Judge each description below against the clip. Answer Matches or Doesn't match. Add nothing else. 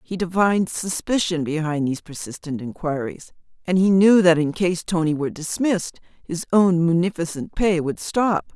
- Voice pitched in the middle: Matches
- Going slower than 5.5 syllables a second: Matches